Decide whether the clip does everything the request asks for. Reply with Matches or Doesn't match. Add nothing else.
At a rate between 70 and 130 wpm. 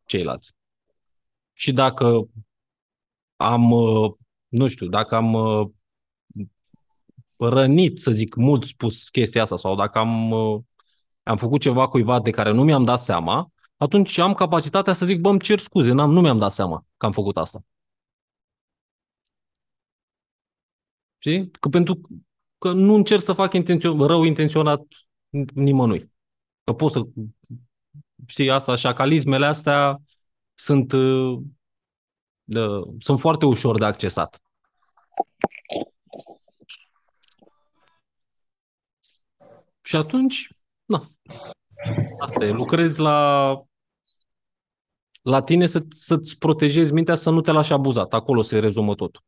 Matches